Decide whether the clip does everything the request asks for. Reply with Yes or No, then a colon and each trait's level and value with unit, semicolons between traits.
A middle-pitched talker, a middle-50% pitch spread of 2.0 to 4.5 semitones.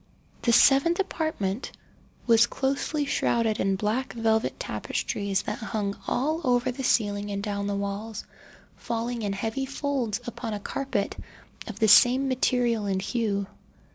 No: high, 230 Hz; average, 4.2 semitones